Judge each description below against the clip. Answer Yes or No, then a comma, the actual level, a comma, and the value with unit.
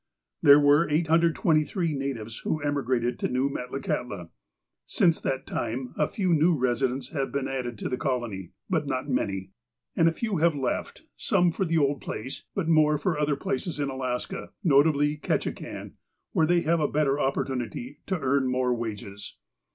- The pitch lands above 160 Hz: No, medium, 140 Hz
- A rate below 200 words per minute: Yes, average, 165 wpm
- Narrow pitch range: No, average, 3.9 semitones